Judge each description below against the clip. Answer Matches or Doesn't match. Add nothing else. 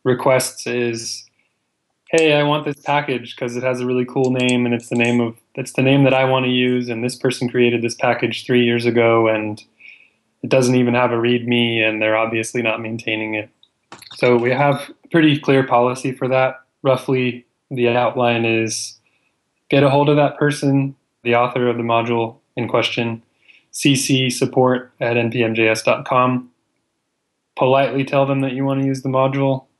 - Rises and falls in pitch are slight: Matches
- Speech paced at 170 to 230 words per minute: Matches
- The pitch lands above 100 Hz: Matches